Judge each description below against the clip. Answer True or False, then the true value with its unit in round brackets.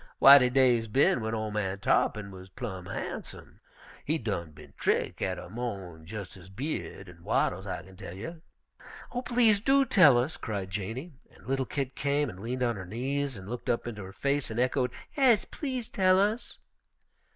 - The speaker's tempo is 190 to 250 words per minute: True (195 wpm)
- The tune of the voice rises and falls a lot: True (6.7 semitones)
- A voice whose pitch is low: True (120 Hz)